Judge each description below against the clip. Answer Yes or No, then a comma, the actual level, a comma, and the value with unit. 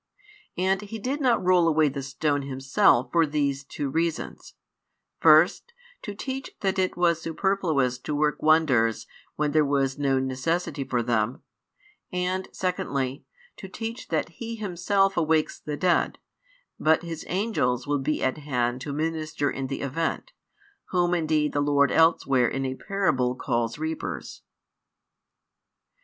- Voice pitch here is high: No, medium, 155 Hz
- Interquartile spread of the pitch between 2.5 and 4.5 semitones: No, average, 5.0 semitones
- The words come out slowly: No, average, 145 wpm